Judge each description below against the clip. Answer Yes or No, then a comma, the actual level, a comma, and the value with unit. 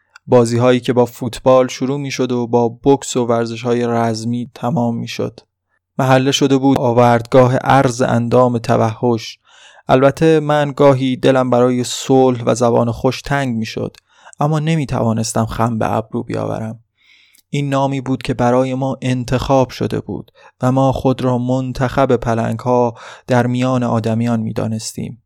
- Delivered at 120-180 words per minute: Yes, fast, 155 wpm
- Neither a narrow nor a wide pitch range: No, narrow, 2.0 semitones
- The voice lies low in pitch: Yes, low, 125 Hz